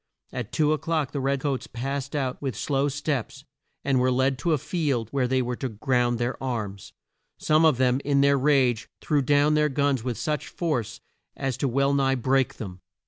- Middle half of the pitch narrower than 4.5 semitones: Yes, narrow, 2.4 semitones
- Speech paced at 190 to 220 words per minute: Yes, average, 195 wpm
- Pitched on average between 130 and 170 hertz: Yes, low, 135 Hz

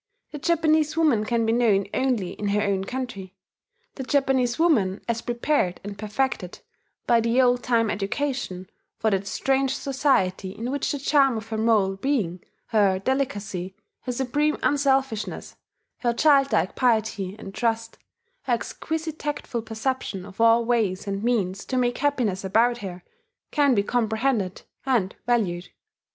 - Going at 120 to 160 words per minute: Yes, average, 150 wpm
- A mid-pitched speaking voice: No, high, 230 Hz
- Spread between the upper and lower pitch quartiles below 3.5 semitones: No, average, 4.9 semitones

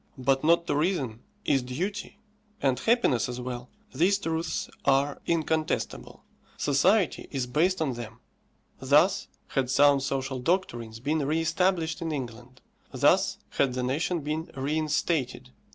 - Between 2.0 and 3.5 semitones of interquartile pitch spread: No, average, 4.3 semitones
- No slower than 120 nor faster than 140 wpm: Yes, slow, 135 wpm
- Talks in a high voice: No, medium, 145 Hz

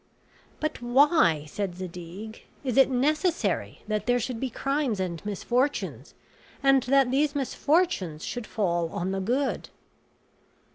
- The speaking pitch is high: Yes, high, 245 Hz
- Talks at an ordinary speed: No, slow, 130 wpm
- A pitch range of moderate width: No, wide, 6.5 semitones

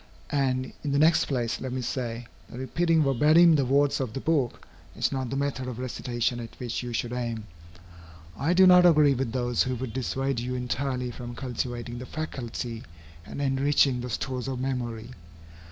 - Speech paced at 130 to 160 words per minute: No, average, 185 wpm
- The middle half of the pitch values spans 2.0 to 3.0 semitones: Yes, narrow, 2.4 semitones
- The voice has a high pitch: No, low, 130 Hz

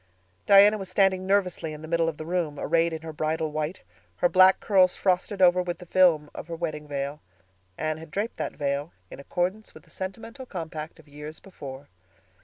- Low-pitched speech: No, medium, 170 Hz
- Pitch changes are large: No, average, 3.4 semitones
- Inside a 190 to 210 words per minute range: Yes, average, 200 wpm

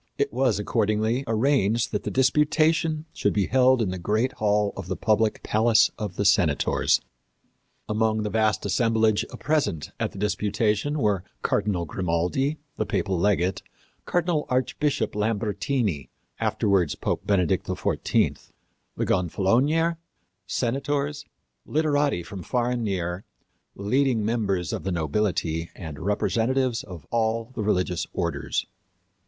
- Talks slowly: Yes, slow, 125 wpm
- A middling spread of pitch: Yes, average, 4.9 semitones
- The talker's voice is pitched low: Yes, low, 110 Hz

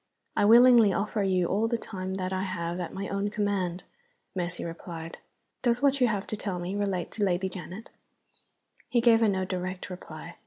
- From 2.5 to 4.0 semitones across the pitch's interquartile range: Yes, average, 2.9 semitones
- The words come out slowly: No, average, 190 wpm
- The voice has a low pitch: No, high, 195 Hz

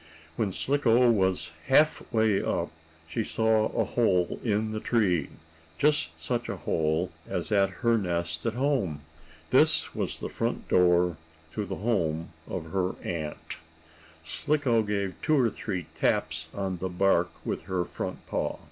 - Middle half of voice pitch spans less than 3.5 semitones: No, average, 4.7 semitones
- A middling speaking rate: Yes, average, 150 wpm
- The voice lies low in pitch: Yes, very low, 95 Hz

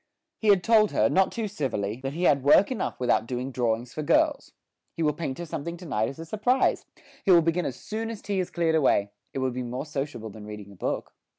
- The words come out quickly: Yes, fast, 240 wpm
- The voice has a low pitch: No, medium, 150 Hz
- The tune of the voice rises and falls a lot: Yes, wide, 7.2 semitones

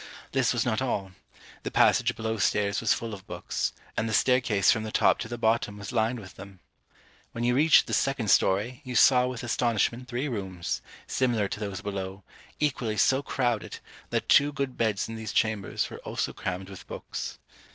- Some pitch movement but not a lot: Yes, average, 3.8 semitones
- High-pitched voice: No, low, 110 Hz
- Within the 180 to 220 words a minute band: Yes, average, 190 wpm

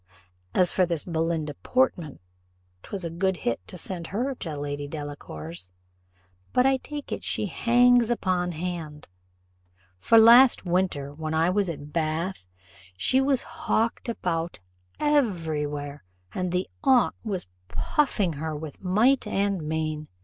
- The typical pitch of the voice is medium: Yes, medium, 175 Hz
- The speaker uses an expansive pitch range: Yes, wide, 6.7 semitones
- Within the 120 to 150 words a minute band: Yes, average, 140 wpm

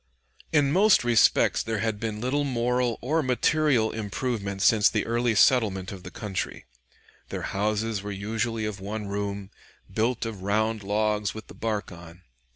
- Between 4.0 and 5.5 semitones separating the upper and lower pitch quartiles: No, average, 2.9 semitones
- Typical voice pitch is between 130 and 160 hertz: No, low, 110 Hz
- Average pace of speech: Yes, average, 160 wpm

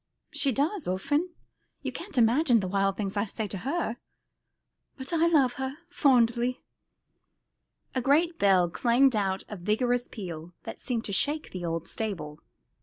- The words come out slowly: No, average, 160 wpm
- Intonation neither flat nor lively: No, wide, 6.0 semitones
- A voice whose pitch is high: Yes, high, 235 Hz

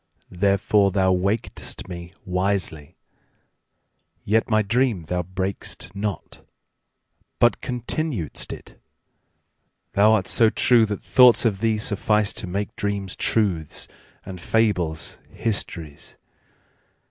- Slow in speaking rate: Yes, slow, 95 wpm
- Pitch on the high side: No, low, 100 Hz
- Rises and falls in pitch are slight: No, average, 3.2 semitones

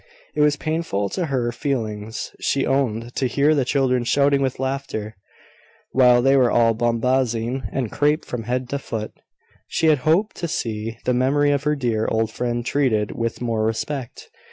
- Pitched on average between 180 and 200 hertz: No, low, 125 Hz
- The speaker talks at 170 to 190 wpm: Yes, average, 175 wpm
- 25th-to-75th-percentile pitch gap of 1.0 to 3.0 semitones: No, average, 3.4 semitones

